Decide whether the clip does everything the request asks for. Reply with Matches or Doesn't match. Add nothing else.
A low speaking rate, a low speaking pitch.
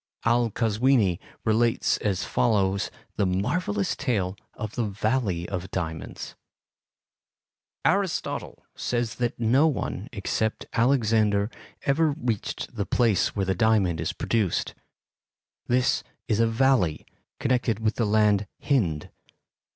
Matches